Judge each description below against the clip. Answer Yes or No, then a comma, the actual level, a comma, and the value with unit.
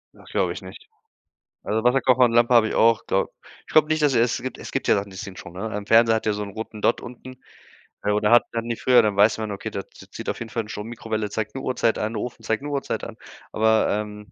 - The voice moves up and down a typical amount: No, narrow, 2.3 semitones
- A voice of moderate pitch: No, low, 110 Hz